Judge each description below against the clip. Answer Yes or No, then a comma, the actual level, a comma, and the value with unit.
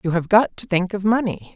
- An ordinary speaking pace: No, fast, 270 wpm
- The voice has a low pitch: No, high, 195 Hz